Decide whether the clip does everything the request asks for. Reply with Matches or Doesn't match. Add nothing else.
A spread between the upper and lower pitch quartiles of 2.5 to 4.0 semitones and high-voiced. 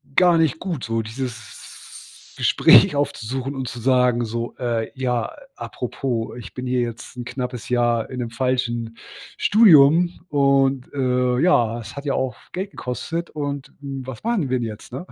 Doesn't match